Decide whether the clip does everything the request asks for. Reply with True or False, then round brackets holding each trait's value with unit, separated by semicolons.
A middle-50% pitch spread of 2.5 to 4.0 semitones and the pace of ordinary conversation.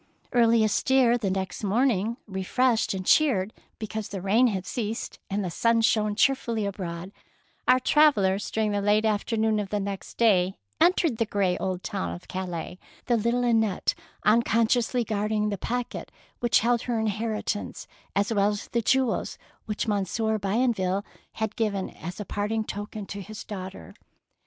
True (2.9 semitones; 160 wpm)